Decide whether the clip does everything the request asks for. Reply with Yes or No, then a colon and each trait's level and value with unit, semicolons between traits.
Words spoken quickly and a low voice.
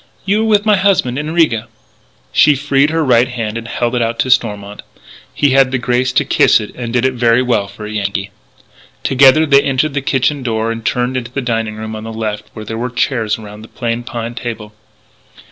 Yes: fast, 215 wpm; low, 120 Hz